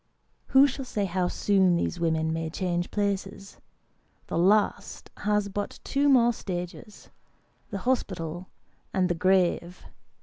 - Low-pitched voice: No, high, 190 Hz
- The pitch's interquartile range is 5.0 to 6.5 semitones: No, average, 3.0 semitones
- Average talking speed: No, slow, 130 wpm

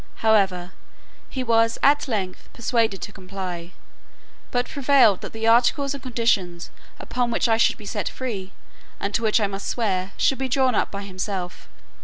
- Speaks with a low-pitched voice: No, high, 220 Hz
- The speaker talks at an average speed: Yes, average, 170 wpm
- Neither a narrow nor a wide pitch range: Yes, average, 4.3 semitones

